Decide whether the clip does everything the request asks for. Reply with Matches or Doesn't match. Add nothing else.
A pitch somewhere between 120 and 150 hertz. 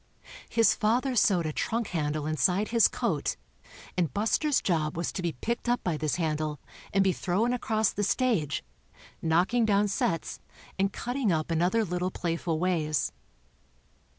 Doesn't match